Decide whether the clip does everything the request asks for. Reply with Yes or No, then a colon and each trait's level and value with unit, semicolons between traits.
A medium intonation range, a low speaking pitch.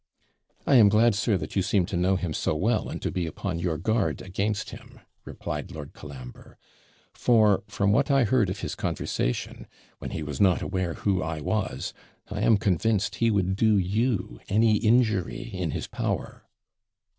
Yes: average, 3.8 semitones; low, 100 Hz